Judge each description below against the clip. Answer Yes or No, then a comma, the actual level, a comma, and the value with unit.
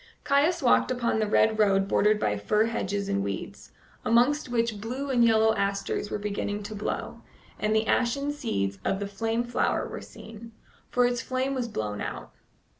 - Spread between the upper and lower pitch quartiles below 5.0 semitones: Yes, average, 3.2 semitones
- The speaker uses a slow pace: No, average, 180 wpm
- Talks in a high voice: Yes, high, 220 Hz